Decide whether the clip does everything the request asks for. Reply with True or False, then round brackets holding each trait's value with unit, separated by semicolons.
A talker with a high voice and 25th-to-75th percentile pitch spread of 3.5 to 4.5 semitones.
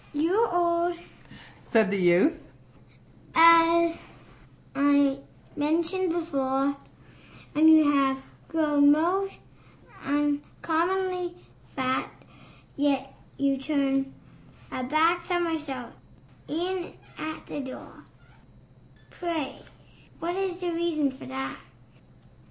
True (310 Hz; 3.8 semitones)